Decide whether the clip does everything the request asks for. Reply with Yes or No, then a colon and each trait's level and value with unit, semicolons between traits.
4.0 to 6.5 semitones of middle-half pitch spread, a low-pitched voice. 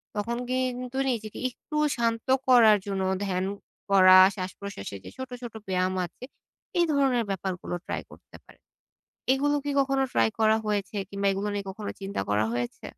No: average, 4.7 semitones; high, 210 Hz